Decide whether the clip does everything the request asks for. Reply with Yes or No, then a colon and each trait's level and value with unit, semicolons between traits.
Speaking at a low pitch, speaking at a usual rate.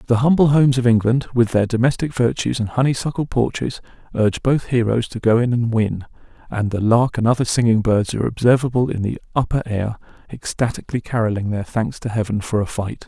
Yes: low, 115 Hz; average, 195 wpm